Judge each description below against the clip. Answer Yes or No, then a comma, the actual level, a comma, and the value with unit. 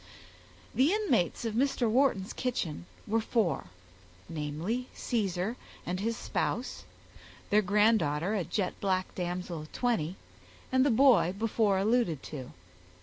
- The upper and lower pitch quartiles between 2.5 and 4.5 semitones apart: No, average, 5.2 semitones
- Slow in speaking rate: Yes, slow, 125 wpm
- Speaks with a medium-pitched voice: No, high, 210 Hz